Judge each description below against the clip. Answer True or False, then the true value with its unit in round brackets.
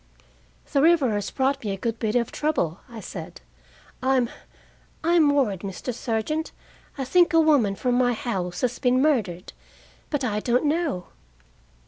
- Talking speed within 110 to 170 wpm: True (155 wpm)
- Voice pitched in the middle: False (250 Hz)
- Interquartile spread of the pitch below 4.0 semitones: False (5.3 semitones)